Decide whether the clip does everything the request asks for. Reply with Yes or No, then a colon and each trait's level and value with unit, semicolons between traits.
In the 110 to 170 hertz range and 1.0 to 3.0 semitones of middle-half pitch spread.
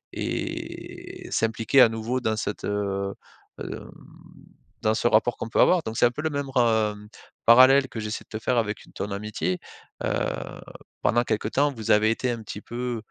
Yes: low, 115 Hz; narrow, 2.6 semitones